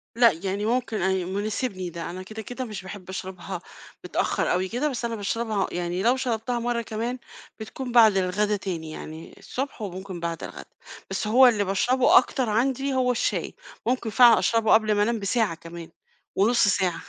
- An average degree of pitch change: Yes, average, 4.2 semitones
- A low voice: No, high, 215 Hz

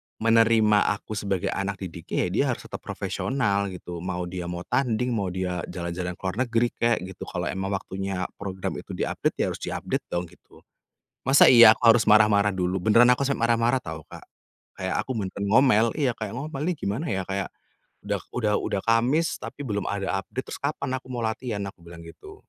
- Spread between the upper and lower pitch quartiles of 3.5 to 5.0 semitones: Yes, average, 4.3 semitones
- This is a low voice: Yes, low, 105 Hz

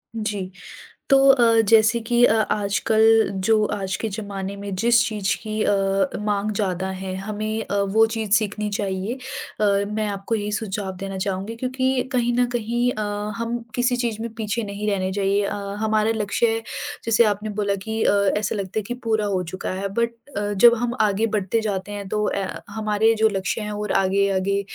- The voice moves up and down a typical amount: No, narrow, 2.2 semitones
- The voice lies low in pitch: No, high, 210 Hz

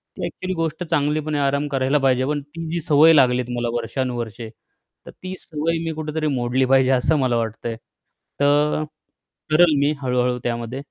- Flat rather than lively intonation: No, average, 3.6 semitones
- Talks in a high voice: No, medium, 140 Hz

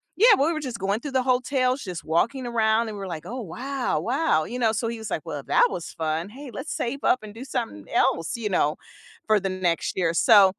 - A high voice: Yes, high, 230 Hz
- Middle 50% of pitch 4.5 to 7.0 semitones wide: Yes, wide, 5.4 semitones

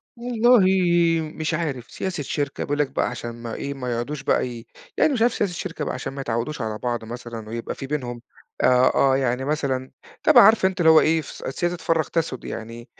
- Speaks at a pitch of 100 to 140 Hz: Yes, low, 135 Hz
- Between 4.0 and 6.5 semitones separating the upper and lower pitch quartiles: Yes, average, 5.1 semitones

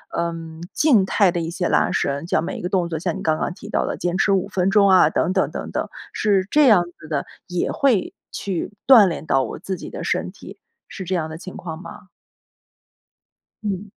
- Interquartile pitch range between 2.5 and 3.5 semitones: Yes, average, 3.1 semitones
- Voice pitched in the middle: Yes, medium, 180 Hz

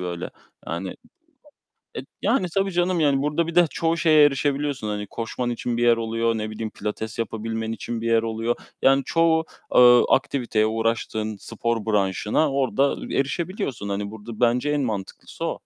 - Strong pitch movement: No, average, 4.7 semitones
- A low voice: Yes, low, 115 Hz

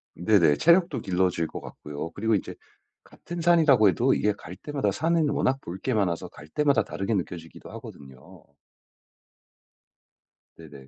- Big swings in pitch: Yes, wide, 9.0 semitones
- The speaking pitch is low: Yes, low, 100 Hz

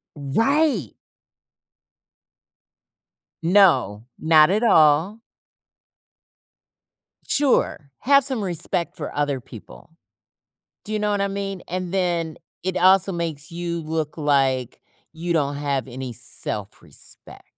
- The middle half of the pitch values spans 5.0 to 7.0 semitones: Yes, wide, 5.5 semitones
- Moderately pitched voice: Yes, medium, 165 Hz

